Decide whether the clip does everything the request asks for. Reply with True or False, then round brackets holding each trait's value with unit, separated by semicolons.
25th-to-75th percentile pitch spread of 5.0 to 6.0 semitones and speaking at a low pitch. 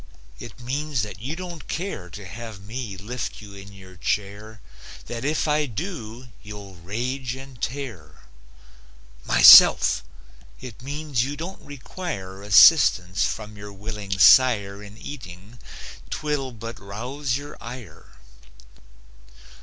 True (5.5 semitones; 115 Hz)